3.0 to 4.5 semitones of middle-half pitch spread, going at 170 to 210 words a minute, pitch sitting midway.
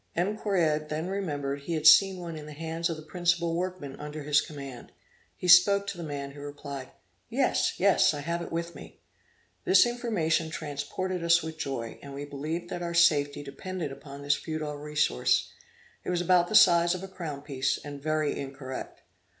Yes: average, 3.4 semitones; average, 190 wpm; medium, 155 Hz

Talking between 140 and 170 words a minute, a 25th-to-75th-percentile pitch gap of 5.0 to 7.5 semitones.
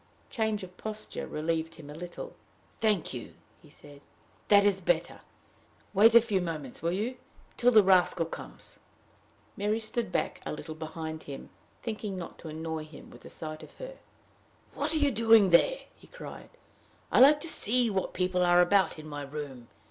No: average, 180 wpm; wide, 5.6 semitones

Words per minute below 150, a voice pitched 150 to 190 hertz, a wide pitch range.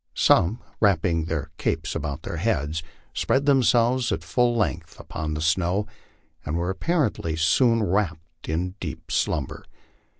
No: slow, 135 wpm; very low, 90 Hz; wide, 6.3 semitones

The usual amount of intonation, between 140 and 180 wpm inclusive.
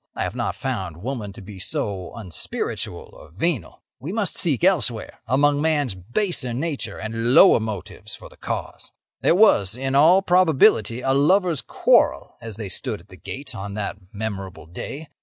No: wide, 6.7 semitones; average, 170 wpm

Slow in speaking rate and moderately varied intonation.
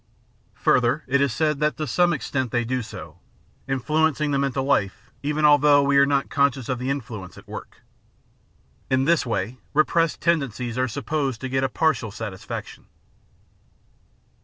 No: average, 160 wpm; average, 3.4 semitones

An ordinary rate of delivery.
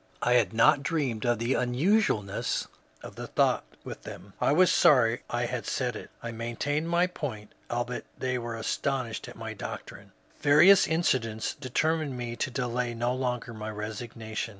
Yes: average, 165 wpm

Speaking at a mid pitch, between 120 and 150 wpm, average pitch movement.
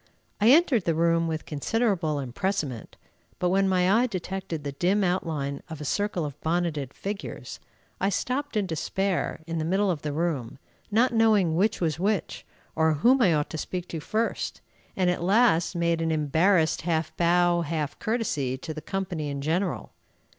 No: medium, 175 Hz; average, 175 wpm; average, 3.8 semitones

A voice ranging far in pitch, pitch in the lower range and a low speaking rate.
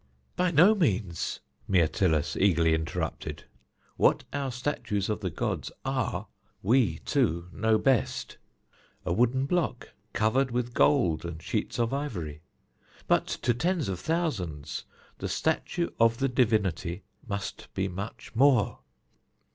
Yes: wide, 7.3 semitones; low, 110 Hz; slow, 125 wpm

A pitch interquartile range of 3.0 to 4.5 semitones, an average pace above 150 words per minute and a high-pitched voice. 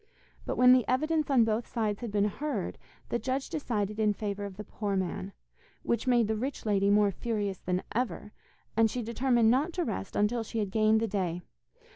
Yes: average, 3.5 semitones; average, 200 wpm; high, 220 Hz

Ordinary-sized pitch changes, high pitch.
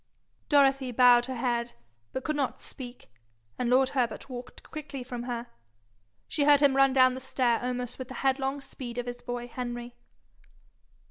No: narrow, 1.8 semitones; very high, 255 Hz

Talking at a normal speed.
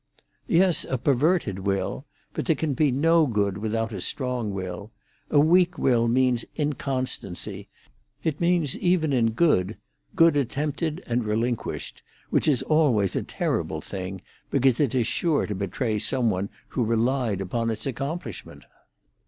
Yes: average, 145 wpm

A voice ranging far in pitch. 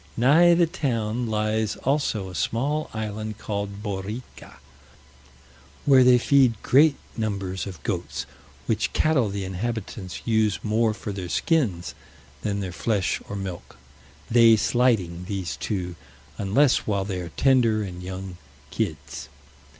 No: average, 4.1 semitones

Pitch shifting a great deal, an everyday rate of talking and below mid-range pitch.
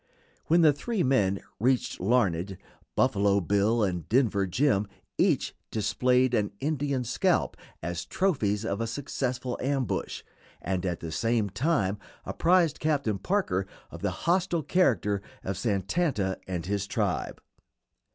No: wide, 6.1 semitones; slow, 130 wpm; low, 115 Hz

